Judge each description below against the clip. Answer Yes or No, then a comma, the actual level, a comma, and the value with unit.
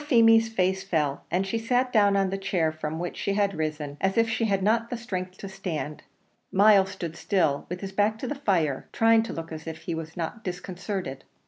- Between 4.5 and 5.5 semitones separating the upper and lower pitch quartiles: Yes, average, 4.9 semitones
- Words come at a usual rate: No, fast, 220 wpm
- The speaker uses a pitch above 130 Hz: Yes, high, 190 Hz